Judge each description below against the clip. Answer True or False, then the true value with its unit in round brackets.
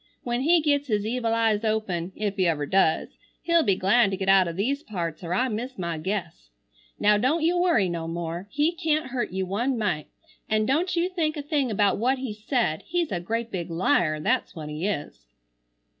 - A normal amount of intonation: False (7.0 semitones)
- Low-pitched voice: False (215 Hz)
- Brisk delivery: True (210 wpm)